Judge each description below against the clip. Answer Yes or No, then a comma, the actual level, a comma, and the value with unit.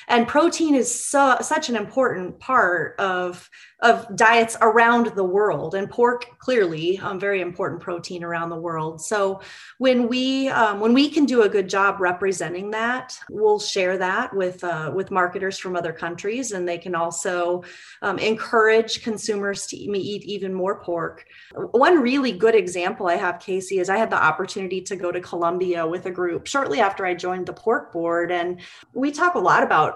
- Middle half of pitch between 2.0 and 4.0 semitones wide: No, average, 4.8 semitones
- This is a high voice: Yes, high, 195 Hz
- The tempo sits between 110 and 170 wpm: No, average, 185 wpm